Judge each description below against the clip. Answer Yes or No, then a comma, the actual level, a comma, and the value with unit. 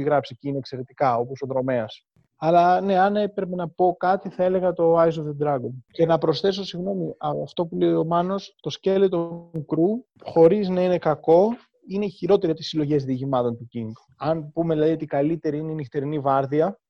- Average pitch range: Yes, average, 4.1 semitones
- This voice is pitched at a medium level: Yes, medium, 165 Hz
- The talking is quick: Yes, fast, 200 wpm